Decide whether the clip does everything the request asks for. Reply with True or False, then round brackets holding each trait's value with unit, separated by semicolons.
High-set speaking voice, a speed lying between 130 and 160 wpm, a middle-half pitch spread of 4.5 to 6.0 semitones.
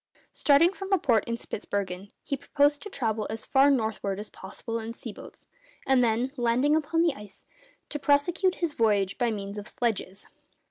False (235 Hz; 180 wpm; 5.4 semitones)